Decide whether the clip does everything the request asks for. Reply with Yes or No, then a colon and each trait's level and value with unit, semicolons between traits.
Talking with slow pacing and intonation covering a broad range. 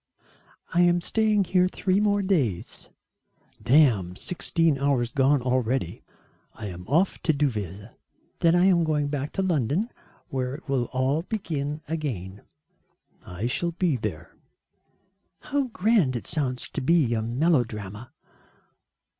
Yes: slow, 130 wpm; wide, 6.4 semitones